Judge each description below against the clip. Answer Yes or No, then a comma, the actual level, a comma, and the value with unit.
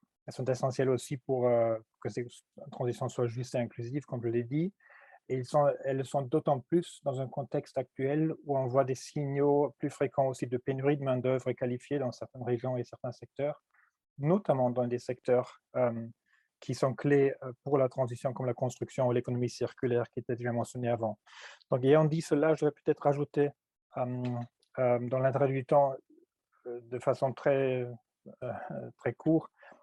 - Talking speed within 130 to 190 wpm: Yes, average, 180 wpm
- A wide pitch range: No, narrow, 2.6 semitones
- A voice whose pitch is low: Yes, low, 130 Hz